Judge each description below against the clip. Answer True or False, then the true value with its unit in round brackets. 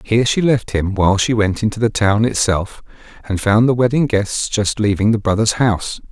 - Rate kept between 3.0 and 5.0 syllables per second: False (5.3 syllables/s)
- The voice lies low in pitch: True (105 Hz)